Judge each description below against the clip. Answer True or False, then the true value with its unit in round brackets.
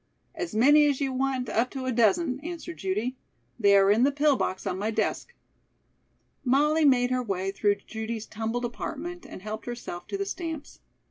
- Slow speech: False (185 wpm)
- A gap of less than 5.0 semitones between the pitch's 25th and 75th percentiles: False (5.3 semitones)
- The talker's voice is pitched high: True (250 Hz)